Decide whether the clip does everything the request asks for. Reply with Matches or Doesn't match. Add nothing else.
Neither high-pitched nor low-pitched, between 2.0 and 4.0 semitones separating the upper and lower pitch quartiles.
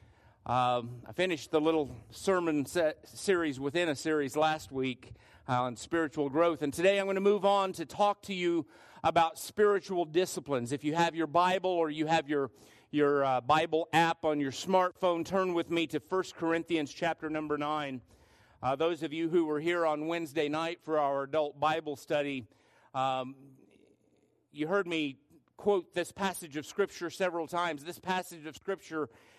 Matches